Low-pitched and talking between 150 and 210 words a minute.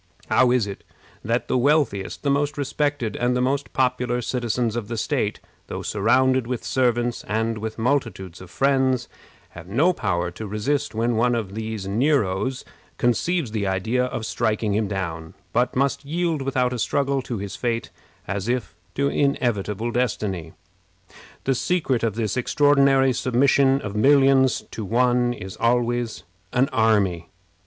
Yes: low, 120 Hz; average, 155 wpm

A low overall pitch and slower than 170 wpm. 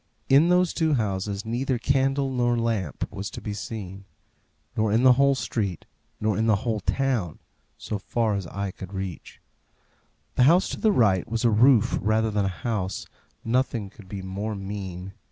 No: low, 110 Hz; average, 175 wpm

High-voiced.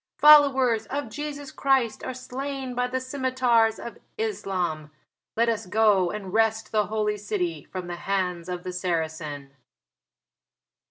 Yes: high, 220 Hz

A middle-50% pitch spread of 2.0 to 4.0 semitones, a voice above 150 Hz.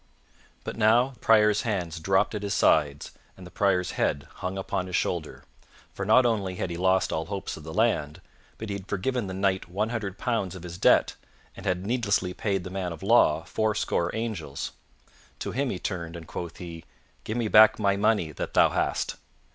No: average, 3.6 semitones; very low, 95 Hz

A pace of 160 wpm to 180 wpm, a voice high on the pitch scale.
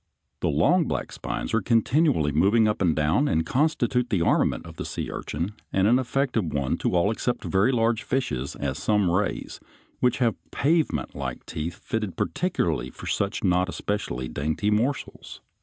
No: average, 165 wpm; low, 105 Hz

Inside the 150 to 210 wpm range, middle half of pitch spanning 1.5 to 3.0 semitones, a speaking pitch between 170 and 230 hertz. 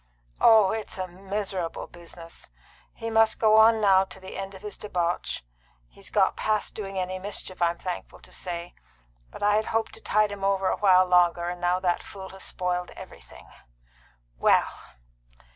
Yes: average, 175 wpm; average, 2.7 semitones; high, 190 Hz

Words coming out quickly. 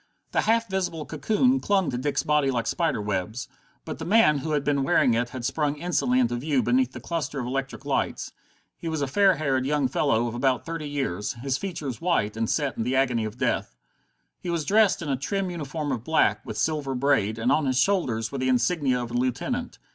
Yes: fast, 220 wpm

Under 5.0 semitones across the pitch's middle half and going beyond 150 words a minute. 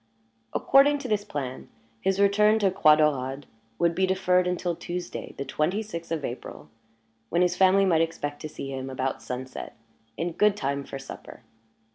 No: wide, 5.5 semitones; average, 170 wpm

